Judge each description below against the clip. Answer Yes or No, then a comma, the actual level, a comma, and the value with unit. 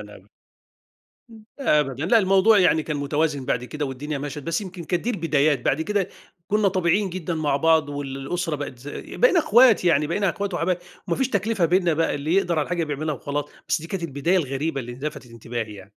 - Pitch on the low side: No, medium, 160 Hz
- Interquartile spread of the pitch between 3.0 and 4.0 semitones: No, average, 4.6 semitones